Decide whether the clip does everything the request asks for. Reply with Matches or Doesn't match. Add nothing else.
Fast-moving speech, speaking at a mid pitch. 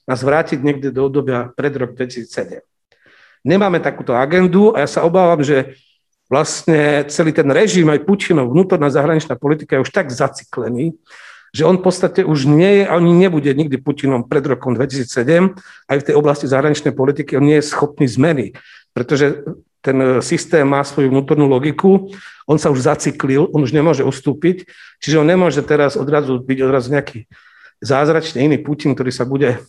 Matches